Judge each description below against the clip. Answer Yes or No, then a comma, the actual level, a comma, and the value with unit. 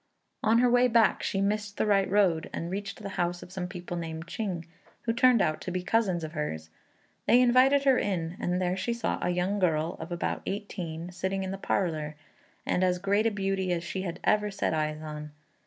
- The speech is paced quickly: Yes, fast, 215 wpm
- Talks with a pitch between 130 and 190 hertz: Yes, medium, 185 Hz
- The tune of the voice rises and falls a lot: No, average, 3.4 semitones